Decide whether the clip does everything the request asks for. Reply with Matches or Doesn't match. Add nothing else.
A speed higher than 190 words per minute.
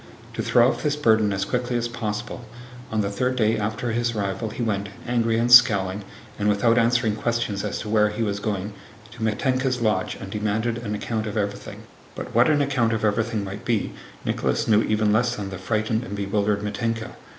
Matches